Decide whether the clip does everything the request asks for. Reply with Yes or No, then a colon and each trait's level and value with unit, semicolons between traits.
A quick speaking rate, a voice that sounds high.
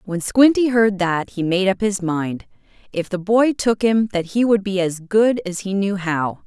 Yes: fast, 225 wpm; high, 200 Hz